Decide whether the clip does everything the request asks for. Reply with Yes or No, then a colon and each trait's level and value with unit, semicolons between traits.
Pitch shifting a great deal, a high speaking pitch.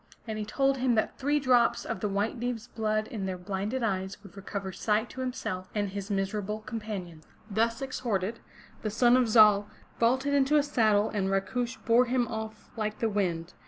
No: average, 3.4 semitones; high, 220 Hz